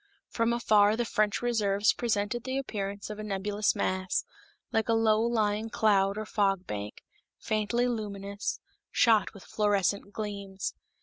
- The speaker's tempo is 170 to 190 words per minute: No, average, 140 wpm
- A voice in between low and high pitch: No, high, 210 Hz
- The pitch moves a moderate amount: No, narrow, 1.9 semitones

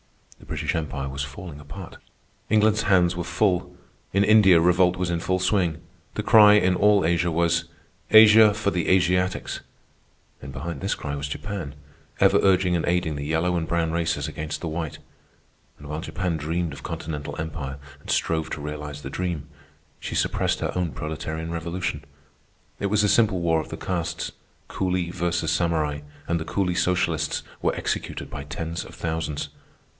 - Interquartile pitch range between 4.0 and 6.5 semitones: No, average, 2.9 semitones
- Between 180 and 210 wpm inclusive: No, average, 170 wpm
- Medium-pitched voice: No, very low, 85 Hz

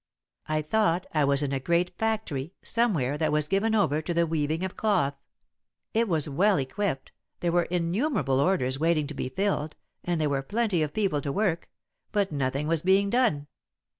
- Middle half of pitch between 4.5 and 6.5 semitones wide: Yes, average, 5.3 semitones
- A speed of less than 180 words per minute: No, average, 185 wpm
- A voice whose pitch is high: No, medium, 165 Hz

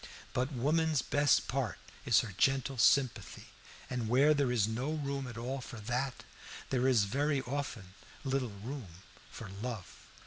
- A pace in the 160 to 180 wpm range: No, average, 150 wpm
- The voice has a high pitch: No, low, 130 Hz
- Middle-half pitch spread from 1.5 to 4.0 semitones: Yes, average, 2.9 semitones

